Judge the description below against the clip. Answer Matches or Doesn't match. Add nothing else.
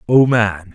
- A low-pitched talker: Matches